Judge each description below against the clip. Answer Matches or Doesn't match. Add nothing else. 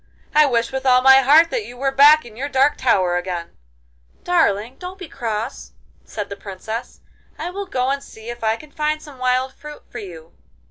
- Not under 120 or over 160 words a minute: Doesn't match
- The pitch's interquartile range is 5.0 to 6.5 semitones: Matches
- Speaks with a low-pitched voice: Doesn't match